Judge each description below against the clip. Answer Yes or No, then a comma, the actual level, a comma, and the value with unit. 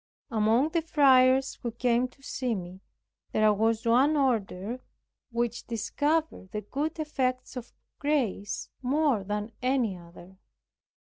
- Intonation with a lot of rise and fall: No, average, 4.3 semitones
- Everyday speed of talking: No, slow, 125 wpm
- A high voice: Yes, high, 245 Hz